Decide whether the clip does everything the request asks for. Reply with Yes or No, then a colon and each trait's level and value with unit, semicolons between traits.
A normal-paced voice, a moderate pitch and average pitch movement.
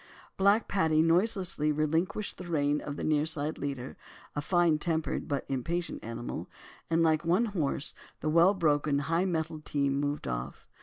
Yes: average, 155 wpm; medium, 155 Hz; average, 3.1 semitones